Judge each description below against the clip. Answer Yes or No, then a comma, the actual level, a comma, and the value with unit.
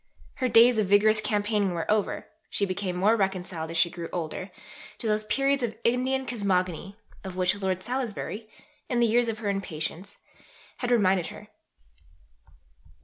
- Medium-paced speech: Yes, average, 155 wpm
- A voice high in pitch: Yes, high, 205 Hz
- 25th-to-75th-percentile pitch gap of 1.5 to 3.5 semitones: No, average, 3.9 semitones